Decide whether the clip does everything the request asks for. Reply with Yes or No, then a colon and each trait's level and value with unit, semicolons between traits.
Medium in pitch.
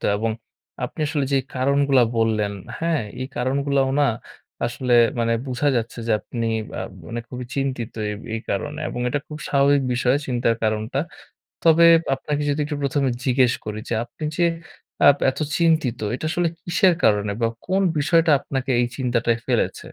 No: low, 130 Hz